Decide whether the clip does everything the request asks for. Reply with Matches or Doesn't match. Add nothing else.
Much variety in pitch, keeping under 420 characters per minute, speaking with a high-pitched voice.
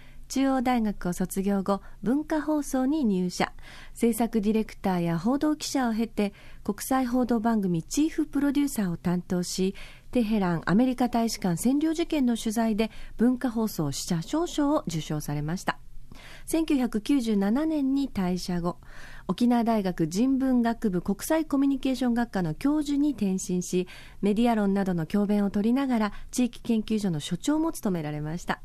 Matches